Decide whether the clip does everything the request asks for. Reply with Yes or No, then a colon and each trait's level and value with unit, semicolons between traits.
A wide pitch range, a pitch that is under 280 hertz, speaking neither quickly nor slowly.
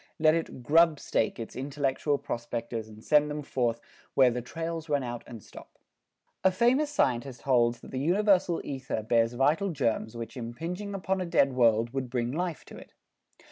Yes: wide, 5.8 semitones; low, 135 Hz; average, 175 wpm